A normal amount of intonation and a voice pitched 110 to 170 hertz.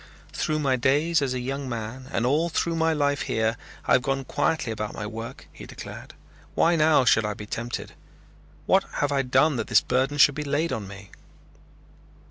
Yes: average, 4.0 semitones; low, 135 Hz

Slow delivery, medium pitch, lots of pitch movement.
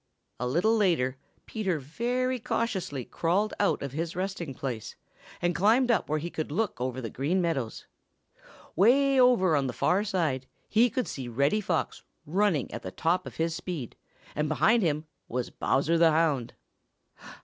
No: average, 165 wpm; medium, 165 Hz; wide, 7.0 semitones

